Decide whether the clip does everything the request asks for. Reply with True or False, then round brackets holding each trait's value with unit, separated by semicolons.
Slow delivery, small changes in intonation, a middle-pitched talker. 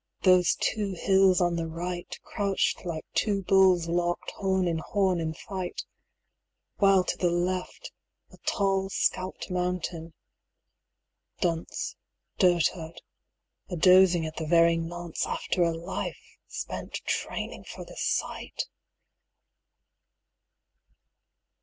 True (110 wpm; 2.1 semitones; 180 Hz)